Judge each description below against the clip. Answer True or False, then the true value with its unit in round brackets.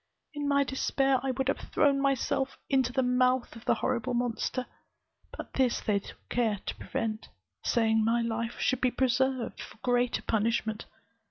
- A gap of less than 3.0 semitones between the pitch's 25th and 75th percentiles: True (2.4 semitones)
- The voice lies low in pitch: False (250 Hz)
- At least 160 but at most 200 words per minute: True (170 wpm)